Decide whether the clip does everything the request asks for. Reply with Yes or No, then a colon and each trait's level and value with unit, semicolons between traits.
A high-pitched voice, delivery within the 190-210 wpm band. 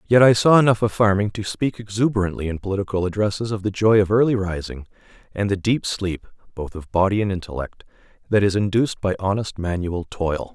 No: low, 100 Hz; average, 195 wpm